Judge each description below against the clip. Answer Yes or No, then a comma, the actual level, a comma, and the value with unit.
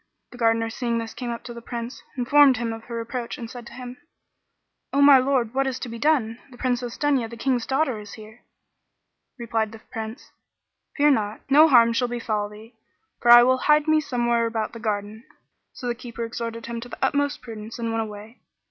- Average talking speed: No, fast, 210 wpm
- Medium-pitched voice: No, high, 235 Hz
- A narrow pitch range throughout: Yes, narrow, 2.2 semitones